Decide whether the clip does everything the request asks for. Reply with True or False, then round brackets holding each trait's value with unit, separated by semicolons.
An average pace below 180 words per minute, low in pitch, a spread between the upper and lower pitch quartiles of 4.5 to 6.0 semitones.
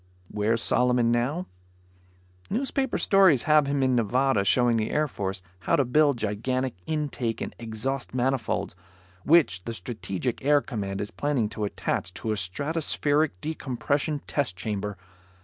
True (140 wpm; 125 Hz; 5.2 semitones)